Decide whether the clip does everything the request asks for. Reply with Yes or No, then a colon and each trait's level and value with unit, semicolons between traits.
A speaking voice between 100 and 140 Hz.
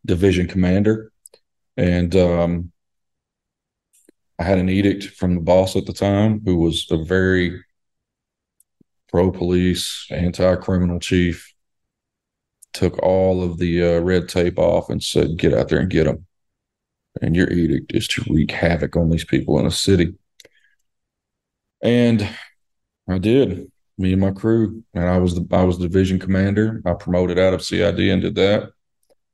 No: very low, 90 Hz